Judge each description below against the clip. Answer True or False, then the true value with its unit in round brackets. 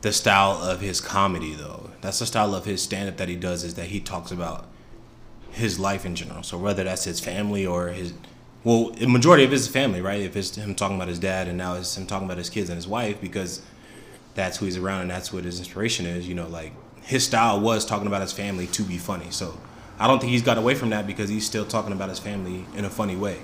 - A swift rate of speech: True (255 wpm)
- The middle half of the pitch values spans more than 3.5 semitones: False (2.9 semitones)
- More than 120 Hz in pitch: False (100 Hz)